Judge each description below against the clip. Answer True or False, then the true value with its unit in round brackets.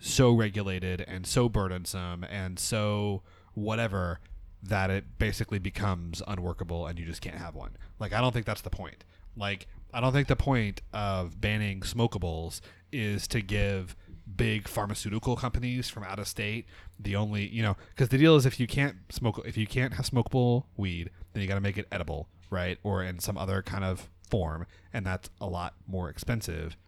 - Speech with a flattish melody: False (3.7 semitones)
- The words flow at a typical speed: True (190 wpm)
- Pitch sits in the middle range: False (100 Hz)